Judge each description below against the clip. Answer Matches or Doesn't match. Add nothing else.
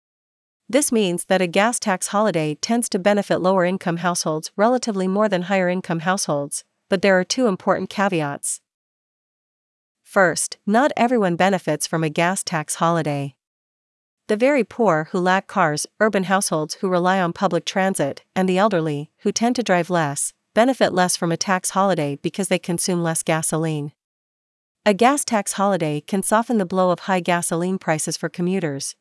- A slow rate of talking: Doesn't match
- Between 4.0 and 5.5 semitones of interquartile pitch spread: Doesn't match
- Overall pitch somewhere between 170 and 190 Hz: Matches